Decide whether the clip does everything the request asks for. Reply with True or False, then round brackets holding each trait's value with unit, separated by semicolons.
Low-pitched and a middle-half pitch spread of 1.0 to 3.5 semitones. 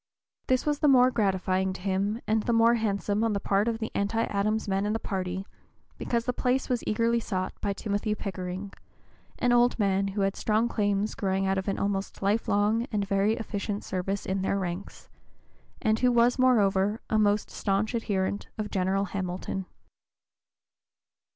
False (205 Hz; 2.7 semitones)